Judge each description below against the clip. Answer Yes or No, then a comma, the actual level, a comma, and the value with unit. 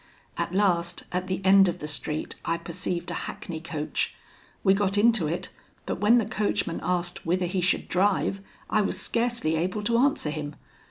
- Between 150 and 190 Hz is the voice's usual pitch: Yes, medium, 185 Hz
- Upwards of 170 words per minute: Yes, average, 180 wpm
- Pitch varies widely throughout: No, average, 3.4 semitones